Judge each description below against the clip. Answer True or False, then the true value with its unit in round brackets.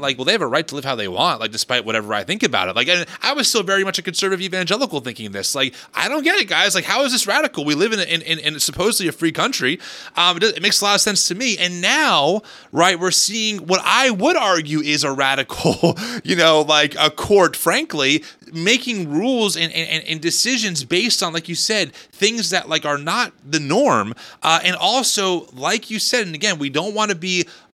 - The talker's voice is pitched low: False (180 Hz)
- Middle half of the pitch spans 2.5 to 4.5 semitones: False (5.6 semitones)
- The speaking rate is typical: False (240 wpm)